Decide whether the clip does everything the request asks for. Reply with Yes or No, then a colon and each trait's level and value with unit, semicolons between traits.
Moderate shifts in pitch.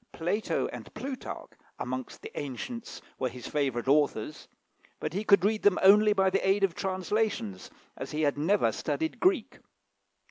No: wide, 6.6 semitones